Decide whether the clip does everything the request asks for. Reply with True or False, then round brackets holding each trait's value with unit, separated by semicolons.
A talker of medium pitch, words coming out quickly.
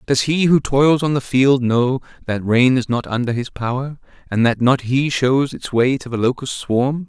False (130 Hz; 220 wpm)